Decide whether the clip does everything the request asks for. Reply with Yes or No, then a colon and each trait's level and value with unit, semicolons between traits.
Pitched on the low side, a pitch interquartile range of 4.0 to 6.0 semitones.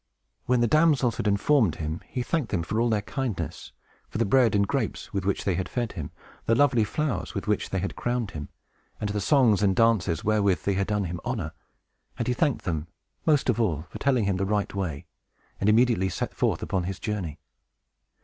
Yes: low, 105 Hz; average, 4.3 semitones